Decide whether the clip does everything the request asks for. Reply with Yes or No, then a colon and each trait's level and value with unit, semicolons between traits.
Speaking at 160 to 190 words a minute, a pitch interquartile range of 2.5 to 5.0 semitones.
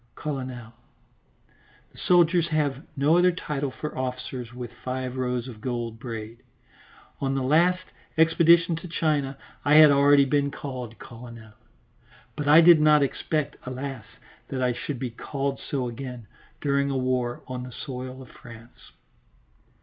No: average, 145 wpm; average, 3.1 semitones